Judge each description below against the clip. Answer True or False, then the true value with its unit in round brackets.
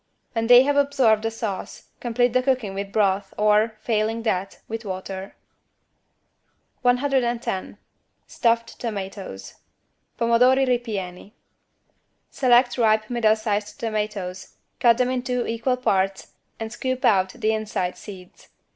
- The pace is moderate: False (120 wpm)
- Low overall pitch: False (225 Hz)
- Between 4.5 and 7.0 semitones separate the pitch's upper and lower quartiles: False (3.4 semitones)